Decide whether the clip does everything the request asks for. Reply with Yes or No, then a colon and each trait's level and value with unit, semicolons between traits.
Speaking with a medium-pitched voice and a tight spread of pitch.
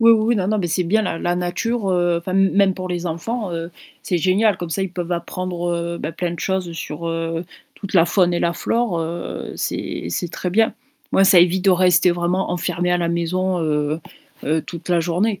Yes: medium, 175 Hz; narrow, 1.9 semitones